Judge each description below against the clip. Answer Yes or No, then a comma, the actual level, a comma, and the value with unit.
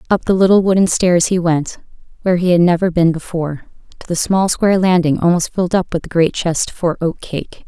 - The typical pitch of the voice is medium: Yes, medium, 175 Hz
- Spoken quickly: Yes, fast, 220 wpm